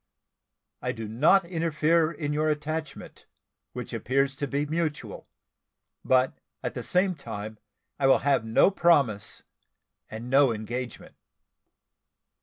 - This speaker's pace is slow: Yes, slow, 120 wpm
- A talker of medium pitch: Yes, medium, 145 Hz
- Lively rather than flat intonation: No, average, 4.5 semitones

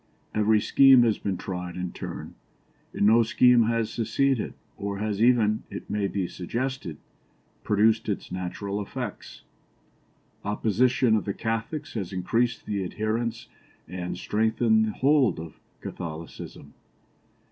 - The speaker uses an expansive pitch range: No, average, 3.1 semitones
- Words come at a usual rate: No, slow, 125 wpm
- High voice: No, low, 110 Hz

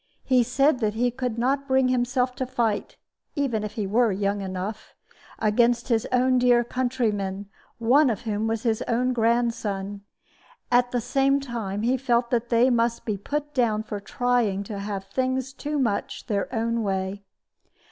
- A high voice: Yes, high, 235 Hz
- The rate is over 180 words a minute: No, average, 165 wpm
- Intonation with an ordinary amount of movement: Yes, average, 3.2 semitones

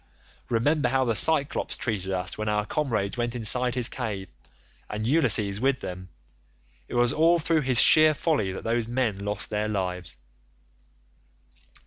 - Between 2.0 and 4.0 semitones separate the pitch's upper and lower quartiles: No, average, 4.4 semitones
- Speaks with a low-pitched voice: Yes, low, 115 Hz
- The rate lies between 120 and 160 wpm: Yes, average, 150 wpm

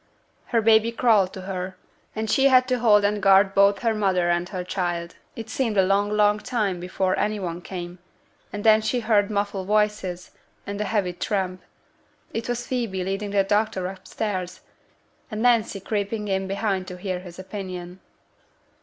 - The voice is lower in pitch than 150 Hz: No, high, 200 Hz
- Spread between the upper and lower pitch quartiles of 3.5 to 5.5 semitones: No, narrow, 2.5 semitones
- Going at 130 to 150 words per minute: No, average, 170 wpm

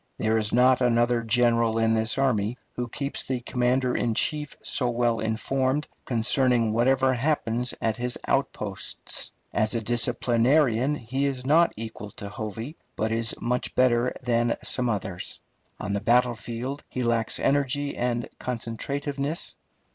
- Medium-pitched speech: No, low, 120 Hz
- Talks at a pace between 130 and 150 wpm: Yes, average, 140 wpm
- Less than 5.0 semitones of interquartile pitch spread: Yes, narrow, 2.4 semitones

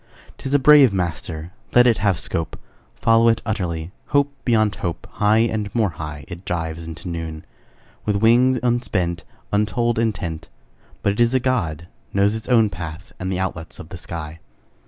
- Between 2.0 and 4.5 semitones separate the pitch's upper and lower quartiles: No, wide, 5.6 semitones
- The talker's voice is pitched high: No, low, 100 Hz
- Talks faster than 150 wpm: Yes, average, 170 wpm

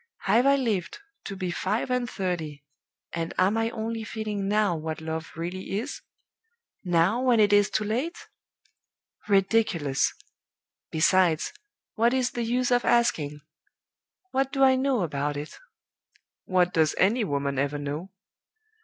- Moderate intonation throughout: No, wide, 6.4 semitones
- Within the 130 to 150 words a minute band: Yes, average, 140 wpm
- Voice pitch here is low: No, high, 195 Hz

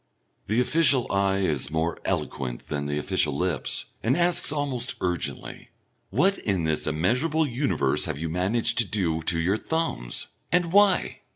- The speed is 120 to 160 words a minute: Yes, average, 155 wpm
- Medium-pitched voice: No, low, 100 Hz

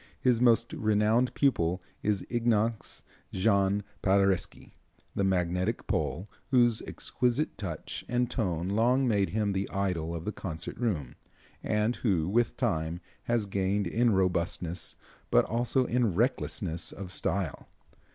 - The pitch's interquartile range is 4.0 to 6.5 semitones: Yes, average, 4.5 semitones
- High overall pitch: No, low, 100 Hz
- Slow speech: Yes, slow, 130 wpm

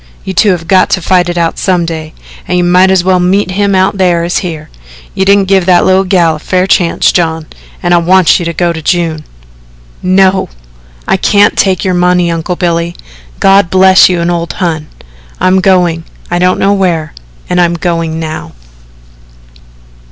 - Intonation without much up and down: Yes, narrow, 2.0 semitones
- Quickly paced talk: No, average, 190 wpm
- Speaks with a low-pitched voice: No, medium, 180 Hz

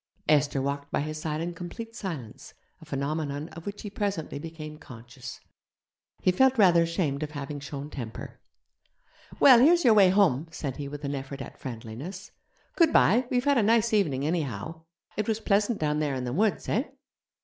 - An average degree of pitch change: No, wide, 6.5 semitones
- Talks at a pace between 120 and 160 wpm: No, average, 180 wpm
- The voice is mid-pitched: Yes, medium, 155 Hz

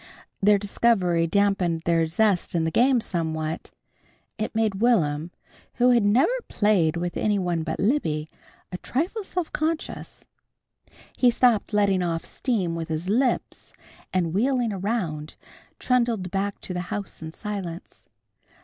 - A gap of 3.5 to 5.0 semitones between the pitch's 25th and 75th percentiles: No, wide, 5.6 semitones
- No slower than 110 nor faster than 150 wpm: Yes, average, 140 wpm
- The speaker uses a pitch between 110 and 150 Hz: No, high, 195 Hz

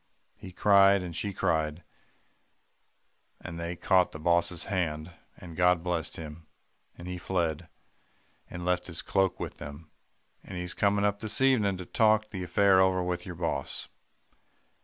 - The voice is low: Yes, very low, 90 Hz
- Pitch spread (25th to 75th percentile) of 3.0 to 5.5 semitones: No, narrow, 2.6 semitones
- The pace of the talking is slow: No, average, 155 wpm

